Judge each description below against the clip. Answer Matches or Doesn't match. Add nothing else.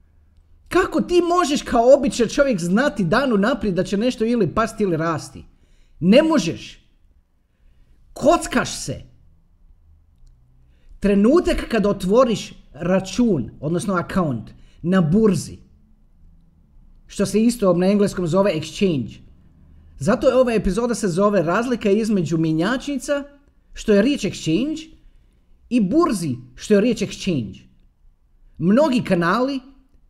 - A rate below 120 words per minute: Matches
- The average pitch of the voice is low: Doesn't match